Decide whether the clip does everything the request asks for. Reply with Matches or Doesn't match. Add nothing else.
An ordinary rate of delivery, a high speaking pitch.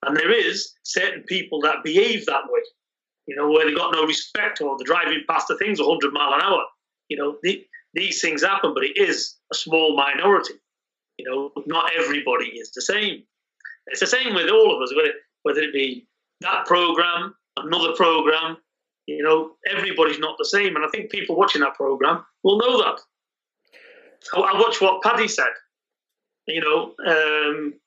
Matches